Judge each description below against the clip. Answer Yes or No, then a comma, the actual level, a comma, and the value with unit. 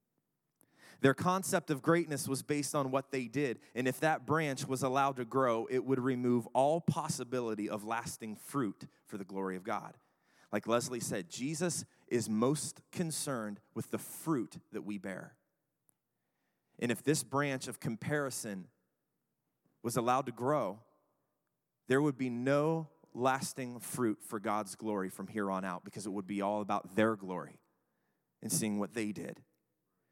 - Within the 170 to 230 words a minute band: No, average, 160 wpm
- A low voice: Yes, low, 125 Hz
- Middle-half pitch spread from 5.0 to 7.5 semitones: Yes, wide, 5.4 semitones